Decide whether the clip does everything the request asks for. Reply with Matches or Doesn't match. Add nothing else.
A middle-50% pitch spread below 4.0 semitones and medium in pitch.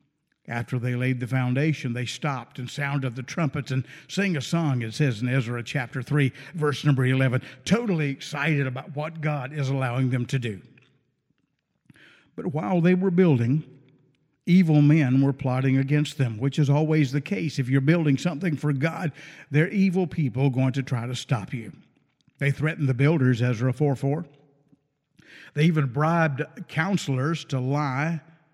Matches